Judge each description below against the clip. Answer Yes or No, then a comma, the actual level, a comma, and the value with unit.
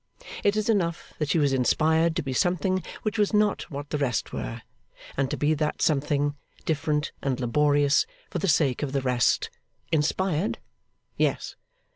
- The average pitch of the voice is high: No, medium, 150 Hz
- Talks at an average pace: Yes, average, 165 wpm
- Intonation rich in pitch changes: No, average, 3.7 semitones